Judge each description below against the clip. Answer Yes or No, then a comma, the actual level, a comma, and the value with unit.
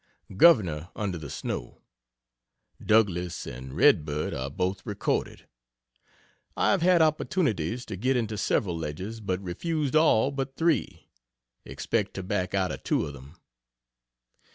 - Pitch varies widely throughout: Yes, wide, 7.7 semitones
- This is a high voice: No, low, 100 Hz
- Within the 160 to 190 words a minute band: No, slow, 135 wpm